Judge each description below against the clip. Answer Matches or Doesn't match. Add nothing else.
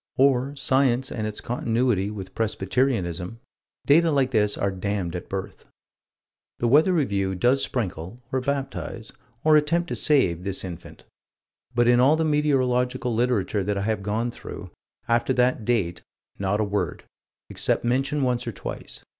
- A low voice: Matches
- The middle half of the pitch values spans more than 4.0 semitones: Matches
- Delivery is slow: Doesn't match